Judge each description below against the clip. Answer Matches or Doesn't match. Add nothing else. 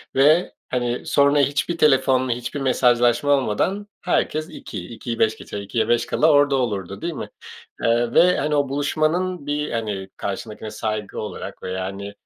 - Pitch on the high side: Doesn't match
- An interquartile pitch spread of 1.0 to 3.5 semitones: Doesn't match